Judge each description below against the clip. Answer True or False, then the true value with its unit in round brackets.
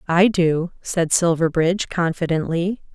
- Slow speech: True (100 wpm)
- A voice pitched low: False (170 Hz)